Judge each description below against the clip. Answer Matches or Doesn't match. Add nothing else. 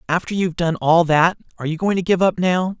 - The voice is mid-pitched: Matches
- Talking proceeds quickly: Matches